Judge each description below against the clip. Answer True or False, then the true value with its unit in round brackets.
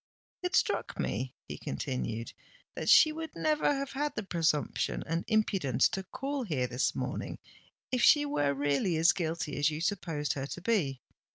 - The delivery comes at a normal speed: True (170 wpm)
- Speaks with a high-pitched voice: False (165 Hz)